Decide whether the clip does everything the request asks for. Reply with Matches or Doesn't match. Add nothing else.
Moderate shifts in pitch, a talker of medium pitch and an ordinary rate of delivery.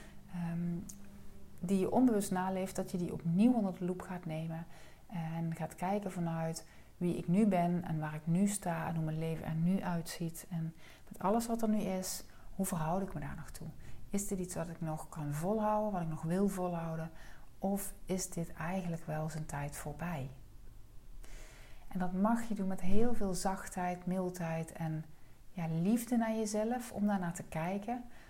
Matches